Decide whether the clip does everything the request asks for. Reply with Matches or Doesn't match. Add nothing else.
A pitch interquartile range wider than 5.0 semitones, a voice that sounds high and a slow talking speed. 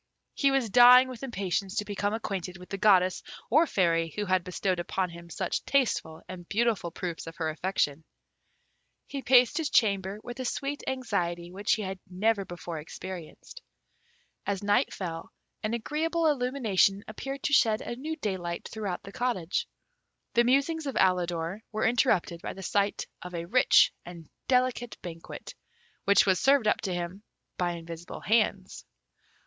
Doesn't match